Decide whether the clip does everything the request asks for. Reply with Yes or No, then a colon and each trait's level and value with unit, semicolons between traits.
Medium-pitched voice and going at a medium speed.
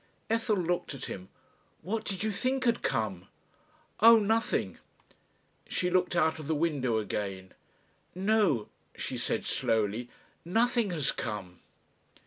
No: medium, 170 Hz; slow, 125 wpm